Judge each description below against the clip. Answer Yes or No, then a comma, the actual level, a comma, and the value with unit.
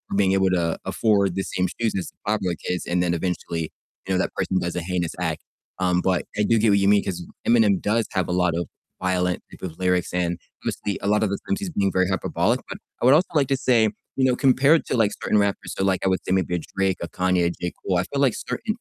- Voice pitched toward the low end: Yes, very low, 95 Hz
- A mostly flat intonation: No, average, 3.0 semitones